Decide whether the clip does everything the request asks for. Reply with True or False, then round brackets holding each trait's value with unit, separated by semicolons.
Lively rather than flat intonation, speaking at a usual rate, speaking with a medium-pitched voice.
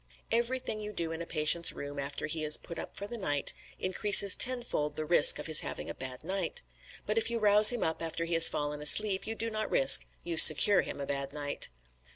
False (6.2 semitones; 225 wpm; 170 Hz)